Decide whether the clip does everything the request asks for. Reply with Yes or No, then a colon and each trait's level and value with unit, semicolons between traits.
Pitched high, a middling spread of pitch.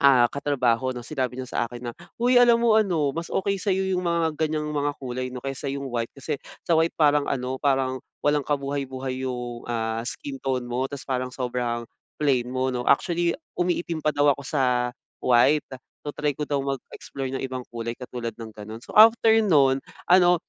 No: low, 135 Hz; average, 3.3 semitones